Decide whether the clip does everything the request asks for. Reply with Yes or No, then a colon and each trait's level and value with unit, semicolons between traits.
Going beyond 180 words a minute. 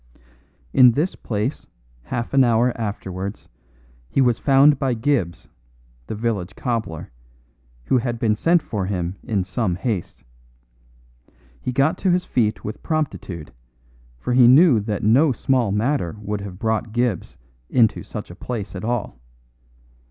No: average, 145 wpm